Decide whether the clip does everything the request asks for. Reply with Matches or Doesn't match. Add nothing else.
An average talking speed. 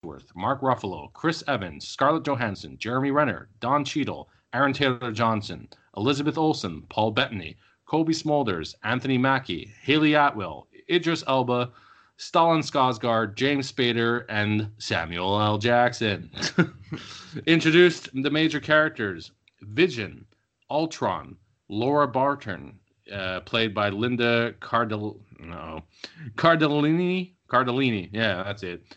Doesn't match